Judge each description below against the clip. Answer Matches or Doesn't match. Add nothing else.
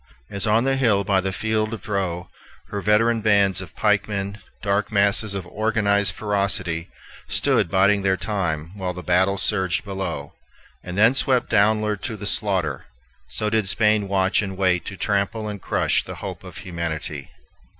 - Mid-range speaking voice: Doesn't match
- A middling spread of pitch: Doesn't match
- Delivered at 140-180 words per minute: Matches